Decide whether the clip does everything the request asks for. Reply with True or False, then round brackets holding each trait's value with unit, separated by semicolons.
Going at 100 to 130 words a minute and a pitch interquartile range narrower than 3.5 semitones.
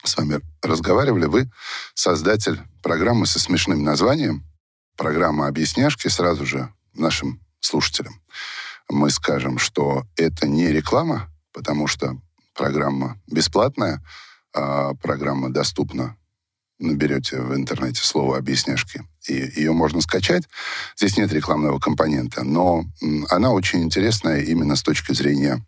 True (115 wpm; 3.1 semitones)